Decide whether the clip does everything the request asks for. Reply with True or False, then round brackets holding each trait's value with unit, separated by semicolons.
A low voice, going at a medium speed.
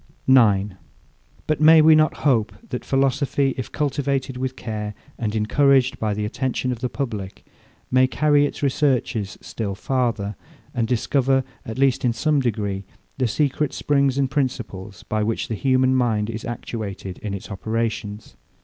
True (125 Hz; 155 wpm)